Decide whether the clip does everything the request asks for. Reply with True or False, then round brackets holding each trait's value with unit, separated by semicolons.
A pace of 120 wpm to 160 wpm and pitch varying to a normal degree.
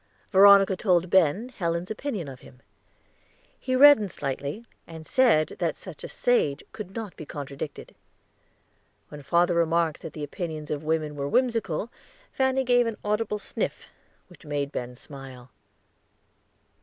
False (140 wpm; 6.5 semitones)